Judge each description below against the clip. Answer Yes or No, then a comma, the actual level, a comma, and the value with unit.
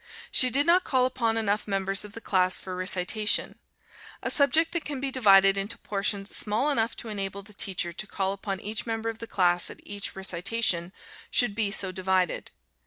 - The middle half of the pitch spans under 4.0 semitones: Yes, average, 3.1 semitones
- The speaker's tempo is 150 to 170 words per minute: No, average, 190 wpm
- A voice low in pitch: No, high, 205 Hz